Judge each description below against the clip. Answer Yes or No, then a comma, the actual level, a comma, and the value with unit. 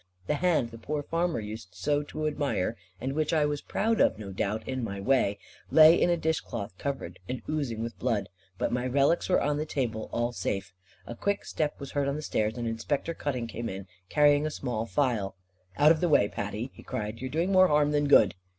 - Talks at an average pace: No, fast, 225 wpm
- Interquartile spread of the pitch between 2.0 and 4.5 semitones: No, average, 5.2 semitones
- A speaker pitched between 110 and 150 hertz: Yes, low, 135 Hz